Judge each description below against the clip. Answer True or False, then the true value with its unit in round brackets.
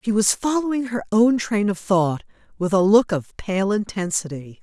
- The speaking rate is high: False (180 wpm)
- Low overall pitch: False (205 Hz)